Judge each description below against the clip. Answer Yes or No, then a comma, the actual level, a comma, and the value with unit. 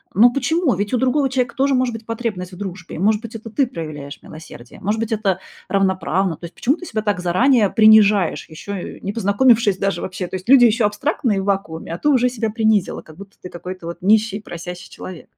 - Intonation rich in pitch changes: No, average, 4.2 semitones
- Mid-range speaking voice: No, high, 205 Hz